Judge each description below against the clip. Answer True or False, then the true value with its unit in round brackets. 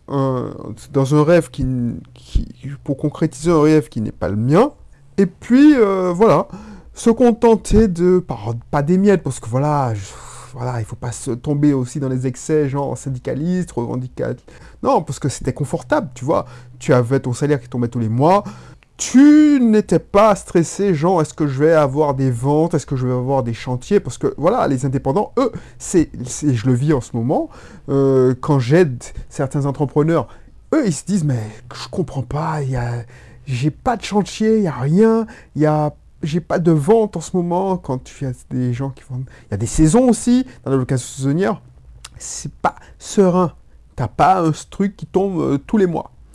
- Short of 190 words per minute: False (200 wpm)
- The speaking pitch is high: False (145 Hz)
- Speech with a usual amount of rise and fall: False (5.9 semitones)